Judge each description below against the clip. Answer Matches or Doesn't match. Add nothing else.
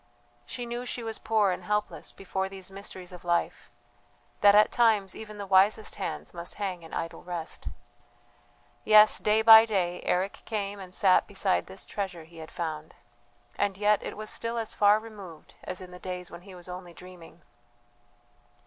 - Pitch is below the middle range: Doesn't match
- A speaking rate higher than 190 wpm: Doesn't match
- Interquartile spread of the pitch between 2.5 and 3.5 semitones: Matches